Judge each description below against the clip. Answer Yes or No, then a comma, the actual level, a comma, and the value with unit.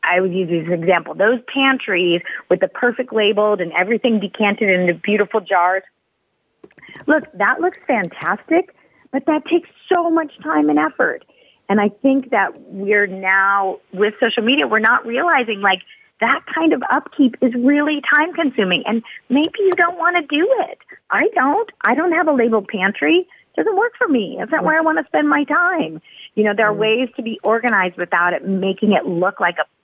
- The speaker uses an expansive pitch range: Yes, wide, 7.6 semitones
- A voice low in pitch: No, high, 220 Hz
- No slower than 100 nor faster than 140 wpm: No, average, 190 wpm